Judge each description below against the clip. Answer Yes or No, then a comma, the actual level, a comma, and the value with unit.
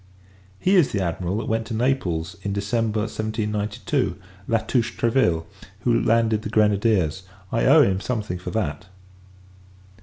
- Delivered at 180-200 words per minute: No, average, 145 wpm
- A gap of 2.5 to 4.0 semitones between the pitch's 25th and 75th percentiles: Yes, average, 2.9 semitones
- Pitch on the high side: No, low, 110 Hz